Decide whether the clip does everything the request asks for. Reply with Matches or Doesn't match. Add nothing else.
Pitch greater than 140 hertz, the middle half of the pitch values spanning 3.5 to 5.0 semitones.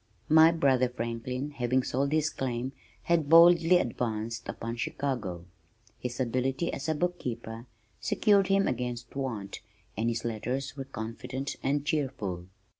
Doesn't match